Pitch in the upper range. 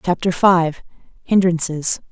No: medium, 175 Hz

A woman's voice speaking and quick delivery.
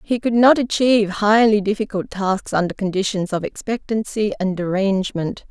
No: female; average, 140 wpm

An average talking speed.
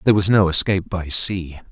No: fast, 210 wpm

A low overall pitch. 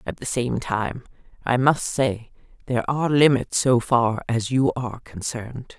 Yes: low, 125 Hz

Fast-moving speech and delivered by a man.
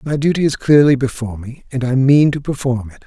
Yes: fast, 235 wpm; male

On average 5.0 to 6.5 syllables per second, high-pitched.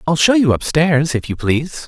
No: 5.2 syllables/s; medium, 155 Hz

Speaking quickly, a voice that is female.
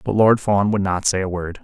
No: fast, 295 wpm; male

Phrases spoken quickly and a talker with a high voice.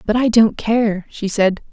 Yes: fast, 210 wpm; high, 215 Hz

